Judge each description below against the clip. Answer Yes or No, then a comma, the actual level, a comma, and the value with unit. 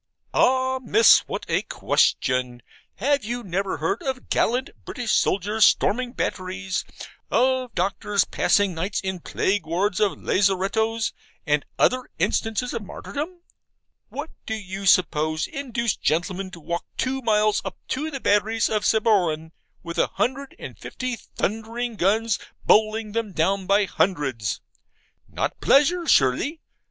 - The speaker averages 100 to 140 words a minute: Yes, slow, 135 wpm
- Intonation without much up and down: No, average, 4.7 semitones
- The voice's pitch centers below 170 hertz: No, high, 210 Hz